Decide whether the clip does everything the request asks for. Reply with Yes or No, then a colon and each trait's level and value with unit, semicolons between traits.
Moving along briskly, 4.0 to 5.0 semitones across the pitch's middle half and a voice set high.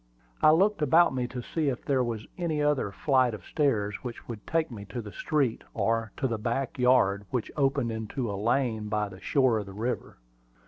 No: fast, 210 wpm; average, 4.4 semitones; low, 125 Hz